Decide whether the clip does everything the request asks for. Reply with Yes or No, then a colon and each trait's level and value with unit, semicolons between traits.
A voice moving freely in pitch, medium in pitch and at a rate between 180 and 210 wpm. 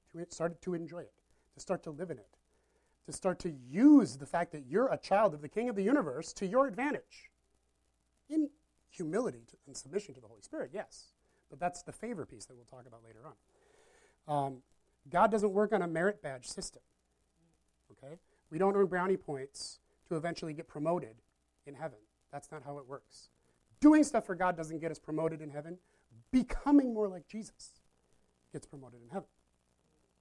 Yes: wide, 7.5 semitones; medium, 165 Hz; average, 185 wpm